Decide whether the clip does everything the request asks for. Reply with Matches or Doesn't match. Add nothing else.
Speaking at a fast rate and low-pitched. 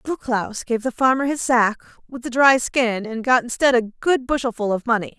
Doesn't match